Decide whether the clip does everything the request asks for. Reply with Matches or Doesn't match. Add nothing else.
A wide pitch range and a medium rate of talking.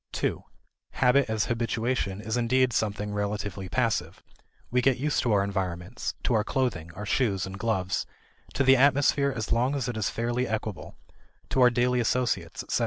Doesn't match